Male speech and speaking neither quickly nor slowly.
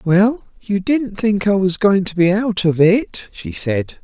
No: male; fast, 210 wpm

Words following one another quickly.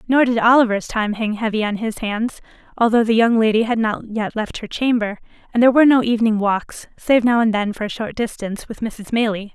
Yes: fast, 225 wpm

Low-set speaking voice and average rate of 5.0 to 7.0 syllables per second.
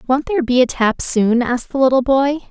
No: very high, 260 Hz; 5.8 syllables/s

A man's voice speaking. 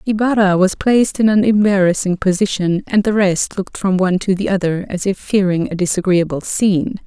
No: female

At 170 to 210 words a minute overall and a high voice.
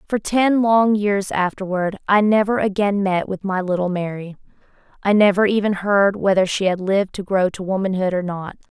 Yes: average, 185 wpm; high, 195 Hz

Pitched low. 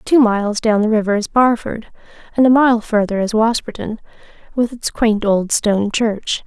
No: high, 220 Hz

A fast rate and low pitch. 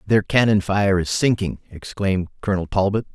No: average, 155 wpm; low, 100 Hz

